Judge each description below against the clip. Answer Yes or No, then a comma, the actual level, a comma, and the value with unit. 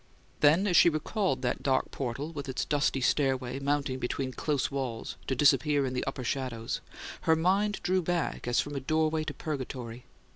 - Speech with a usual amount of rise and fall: Yes, average, 3.3 semitones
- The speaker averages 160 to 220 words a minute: Yes, average, 180 wpm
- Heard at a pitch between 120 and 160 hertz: Yes, medium, 140 Hz